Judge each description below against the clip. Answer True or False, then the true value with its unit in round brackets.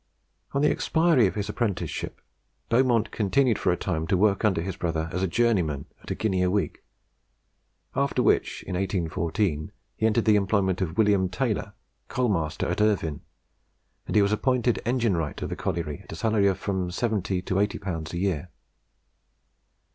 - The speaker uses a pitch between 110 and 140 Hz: False (95 Hz)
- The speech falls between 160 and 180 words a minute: True (170 wpm)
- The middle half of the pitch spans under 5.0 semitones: True (3.9 semitones)